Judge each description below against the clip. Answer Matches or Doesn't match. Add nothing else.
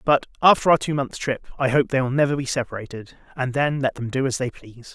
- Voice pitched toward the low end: Matches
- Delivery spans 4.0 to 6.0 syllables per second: Doesn't match